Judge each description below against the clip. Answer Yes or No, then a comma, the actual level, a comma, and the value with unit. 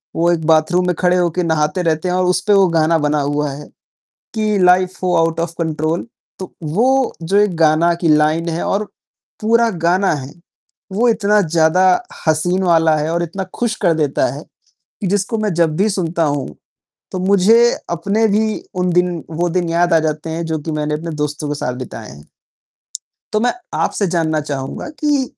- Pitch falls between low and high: Yes, medium, 170 Hz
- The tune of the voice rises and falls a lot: No, average, 3.5 semitones